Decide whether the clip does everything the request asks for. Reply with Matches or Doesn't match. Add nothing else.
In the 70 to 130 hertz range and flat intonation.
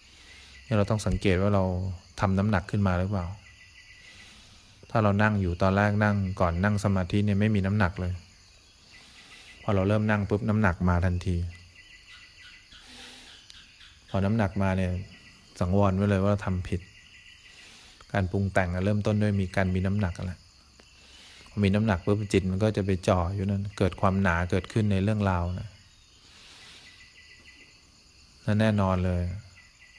Matches